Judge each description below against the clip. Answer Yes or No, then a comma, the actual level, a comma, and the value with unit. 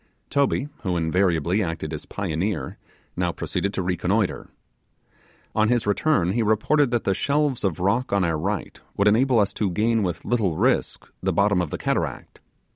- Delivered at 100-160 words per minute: No, average, 170 wpm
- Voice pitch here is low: Yes, low, 100 Hz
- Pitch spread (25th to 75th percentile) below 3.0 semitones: No, average, 4.5 semitones